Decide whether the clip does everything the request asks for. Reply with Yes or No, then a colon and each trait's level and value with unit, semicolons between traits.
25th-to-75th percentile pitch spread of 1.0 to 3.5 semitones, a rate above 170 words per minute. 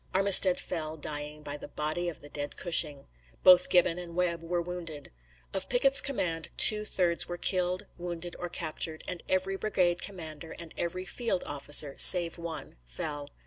No: average, 2.8 semitones; average, 165 wpm